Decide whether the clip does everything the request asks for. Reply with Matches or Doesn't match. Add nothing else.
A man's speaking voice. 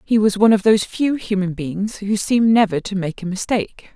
Doesn't match